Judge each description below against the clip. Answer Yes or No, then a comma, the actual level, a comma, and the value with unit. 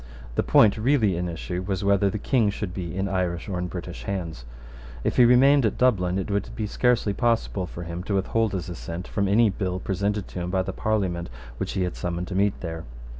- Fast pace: Yes, fast, 225 wpm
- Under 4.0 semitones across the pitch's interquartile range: Yes, average, 2.9 semitones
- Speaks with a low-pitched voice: Yes, very low, 95 Hz